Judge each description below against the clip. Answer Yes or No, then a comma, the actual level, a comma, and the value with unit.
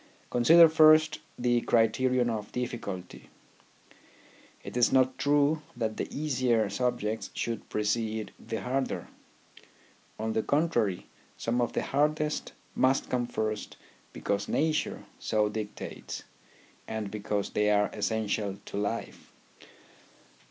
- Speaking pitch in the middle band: No, low, 120 Hz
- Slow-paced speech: Yes, slow, 115 wpm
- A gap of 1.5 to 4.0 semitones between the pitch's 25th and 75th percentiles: Yes, average, 3.7 semitones